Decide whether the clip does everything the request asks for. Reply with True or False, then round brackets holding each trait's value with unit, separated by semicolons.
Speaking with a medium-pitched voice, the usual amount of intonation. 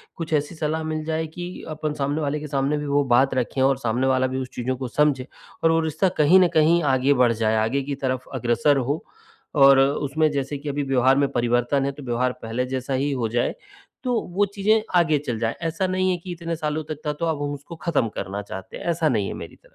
True (145 Hz; 3.5 semitones)